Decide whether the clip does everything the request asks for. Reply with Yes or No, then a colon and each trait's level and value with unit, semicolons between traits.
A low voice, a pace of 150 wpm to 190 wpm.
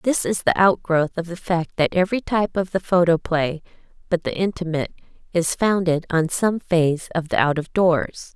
No: medium, 175 Hz; average, 185 wpm